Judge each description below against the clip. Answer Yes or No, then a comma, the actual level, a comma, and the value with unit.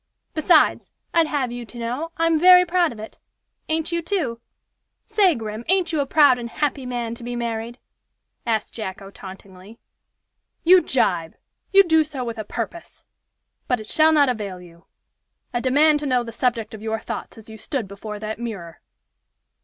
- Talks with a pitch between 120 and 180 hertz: No, high, 240 Hz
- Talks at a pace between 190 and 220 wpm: No, average, 175 wpm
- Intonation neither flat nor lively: No, wide, 6.1 semitones